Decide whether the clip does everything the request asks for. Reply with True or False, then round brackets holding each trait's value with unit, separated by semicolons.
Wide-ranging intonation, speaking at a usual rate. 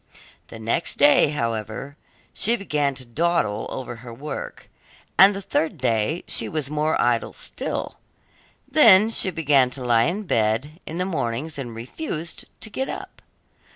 True (6.4 semitones; 155 wpm)